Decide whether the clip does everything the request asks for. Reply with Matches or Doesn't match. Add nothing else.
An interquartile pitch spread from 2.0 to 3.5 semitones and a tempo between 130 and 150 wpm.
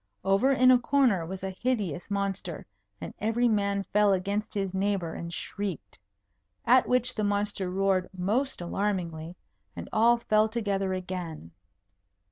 Matches